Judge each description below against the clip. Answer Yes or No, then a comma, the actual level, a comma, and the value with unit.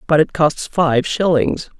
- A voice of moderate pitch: Yes, medium, 155 Hz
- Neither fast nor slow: Yes, average, 165 wpm